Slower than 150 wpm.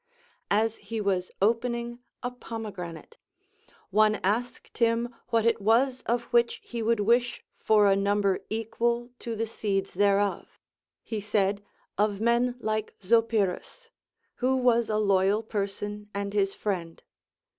Yes: slow, 135 wpm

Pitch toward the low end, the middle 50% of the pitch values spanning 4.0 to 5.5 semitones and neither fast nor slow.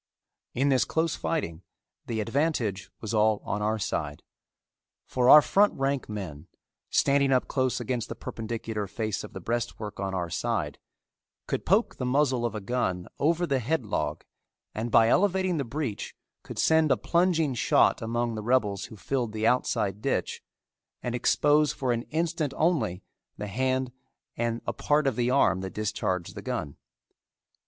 Yes: low, 120 Hz; average, 5.0 semitones; average, 165 wpm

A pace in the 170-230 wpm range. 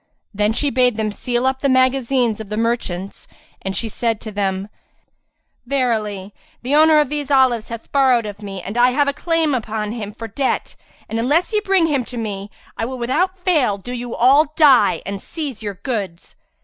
Yes: average, 190 wpm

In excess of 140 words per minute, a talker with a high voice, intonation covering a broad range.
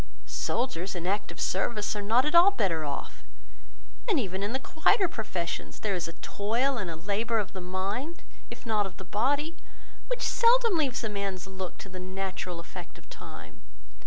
Yes: average, 185 wpm; high, 205 Hz; wide, 6.0 semitones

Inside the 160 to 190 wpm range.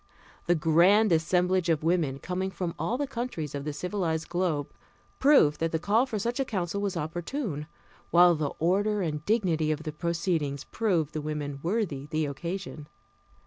Yes: average, 170 wpm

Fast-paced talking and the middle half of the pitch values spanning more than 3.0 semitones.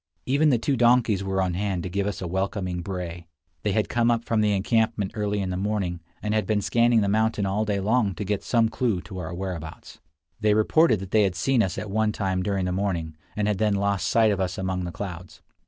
No: fast, 240 wpm; average, 2.7 semitones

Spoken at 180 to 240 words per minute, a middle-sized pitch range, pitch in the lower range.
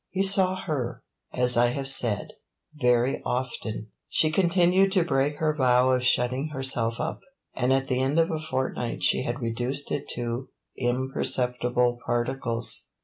No: average, 150 wpm; average, 3.8 semitones; low, 130 Hz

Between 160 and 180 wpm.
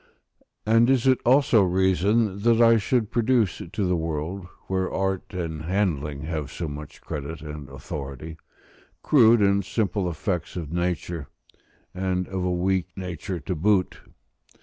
No: average, 145 wpm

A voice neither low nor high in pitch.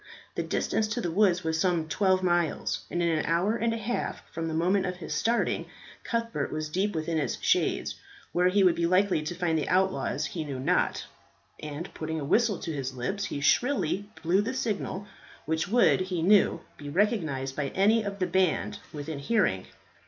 Yes: medium, 175 Hz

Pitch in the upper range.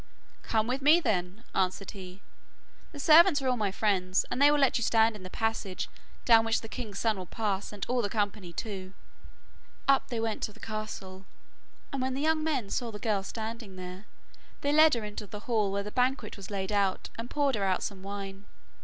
Yes: high, 215 Hz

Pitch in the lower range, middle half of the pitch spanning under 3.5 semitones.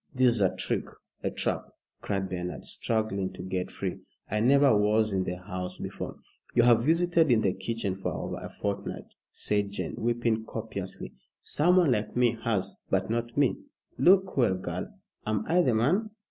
No: low, 110 Hz; average, 4.4 semitones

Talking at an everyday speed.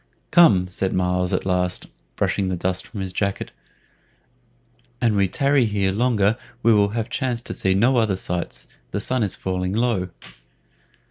Yes: average, 160 wpm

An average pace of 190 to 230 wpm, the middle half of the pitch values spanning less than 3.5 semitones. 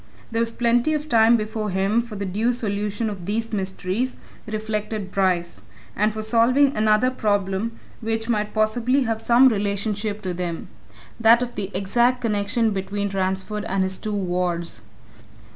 No: average, 155 wpm; average, 2.8 semitones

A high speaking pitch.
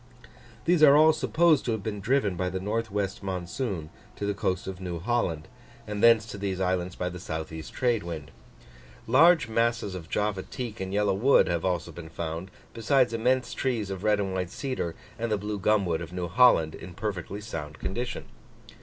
No: low, 100 Hz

